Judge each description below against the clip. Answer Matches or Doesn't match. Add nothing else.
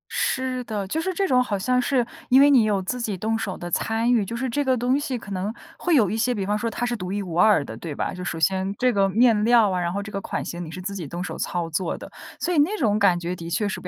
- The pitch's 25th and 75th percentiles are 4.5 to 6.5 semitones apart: Matches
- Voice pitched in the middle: Doesn't match